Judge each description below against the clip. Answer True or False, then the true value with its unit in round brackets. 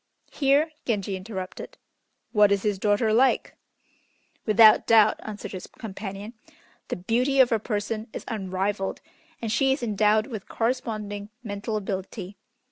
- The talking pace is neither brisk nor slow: False (130 wpm)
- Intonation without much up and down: True (2.2 semitones)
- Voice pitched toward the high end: True (215 Hz)